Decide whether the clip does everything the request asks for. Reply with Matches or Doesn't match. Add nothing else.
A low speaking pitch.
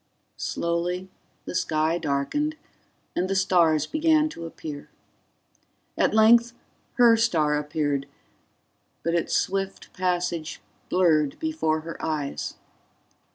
Doesn't match